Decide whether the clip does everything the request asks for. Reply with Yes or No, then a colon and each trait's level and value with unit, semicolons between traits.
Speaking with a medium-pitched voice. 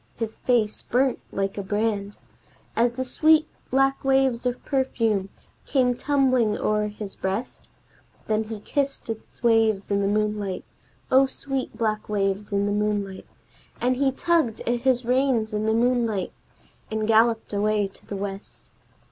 No: high, 225 Hz